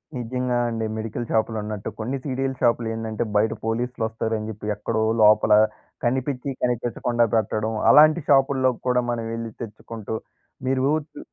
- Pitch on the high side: No, low, 115 Hz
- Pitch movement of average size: No, narrow, 2.3 semitones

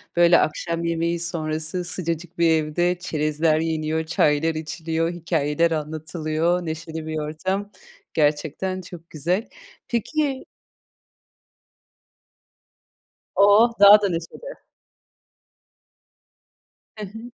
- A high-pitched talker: No, medium, 165 Hz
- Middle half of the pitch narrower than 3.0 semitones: Yes, narrow, 2.5 semitones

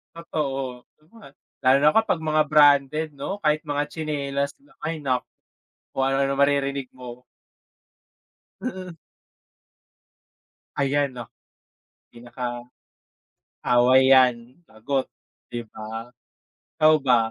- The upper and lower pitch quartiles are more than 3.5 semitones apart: No, average, 3.2 semitones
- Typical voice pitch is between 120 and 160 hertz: Yes, medium, 140 Hz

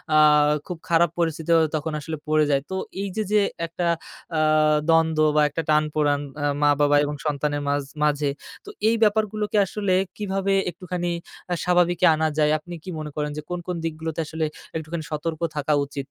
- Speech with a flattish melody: No, average, 3.0 semitones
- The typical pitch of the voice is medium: Yes, medium, 160 Hz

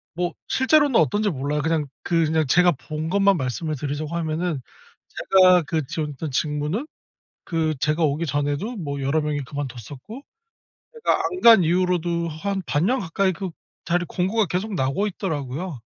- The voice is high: No, medium, 165 Hz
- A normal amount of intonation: Yes, average, 4.2 semitones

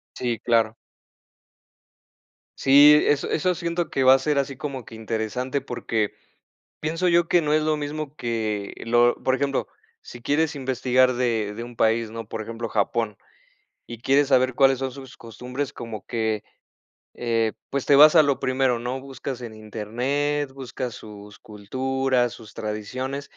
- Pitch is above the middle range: No, low, 130 Hz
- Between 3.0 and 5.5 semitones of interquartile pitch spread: Yes, average, 3.5 semitones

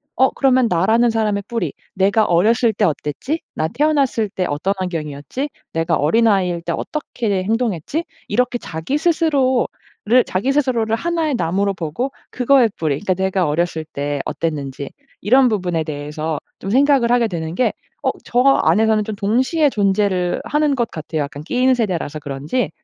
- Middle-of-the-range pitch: No, high, 205 Hz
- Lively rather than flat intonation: Yes, wide, 7.3 semitones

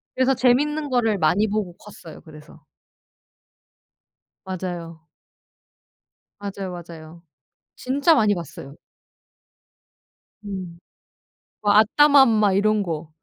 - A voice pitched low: No, high, 200 Hz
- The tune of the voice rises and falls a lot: Yes, wide, 5.7 semitones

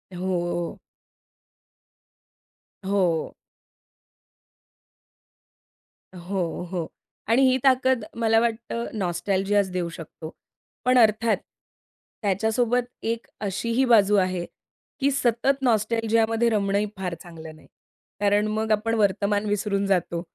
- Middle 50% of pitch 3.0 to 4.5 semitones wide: Yes, average, 3.5 semitones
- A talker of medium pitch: No, high, 210 Hz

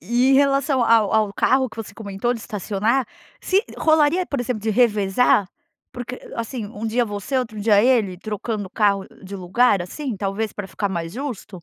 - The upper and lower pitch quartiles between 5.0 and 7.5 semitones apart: No, average, 3.8 semitones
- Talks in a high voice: Yes, high, 220 Hz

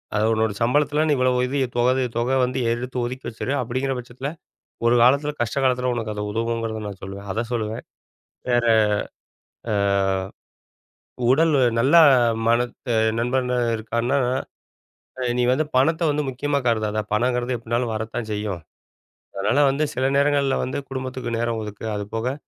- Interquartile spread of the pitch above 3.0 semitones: No, average, 2.7 semitones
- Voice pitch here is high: No, low, 120 Hz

